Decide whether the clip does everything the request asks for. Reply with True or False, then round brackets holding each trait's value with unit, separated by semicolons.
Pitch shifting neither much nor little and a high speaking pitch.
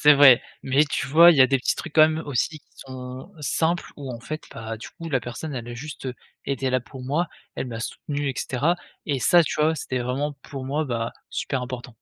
False (3.2 semitones; 135 Hz)